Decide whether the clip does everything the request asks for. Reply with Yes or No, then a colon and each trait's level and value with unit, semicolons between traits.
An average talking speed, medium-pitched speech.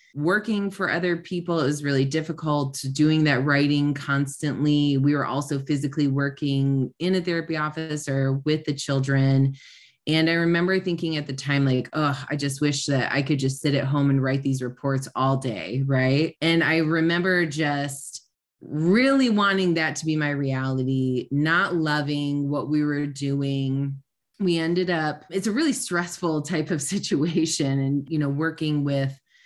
Yes: average, 165 wpm; medium, 145 Hz